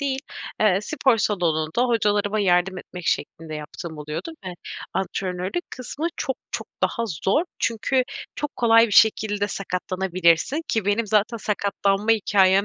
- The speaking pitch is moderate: No, high, 205 Hz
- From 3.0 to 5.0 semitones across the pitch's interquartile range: Yes, average, 3.9 semitones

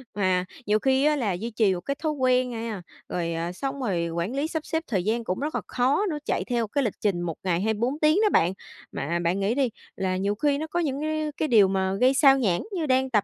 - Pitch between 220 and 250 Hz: Yes, high, 235 Hz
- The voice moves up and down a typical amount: No, wide, 6.8 semitones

